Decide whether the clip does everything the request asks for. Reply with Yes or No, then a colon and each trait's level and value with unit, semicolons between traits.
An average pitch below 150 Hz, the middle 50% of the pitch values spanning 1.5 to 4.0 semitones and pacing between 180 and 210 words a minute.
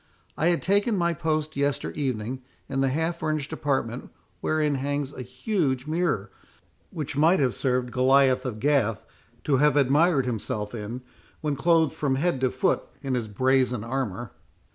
No: low, 135 Hz; average, 3.5 semitones; average, 160 wpm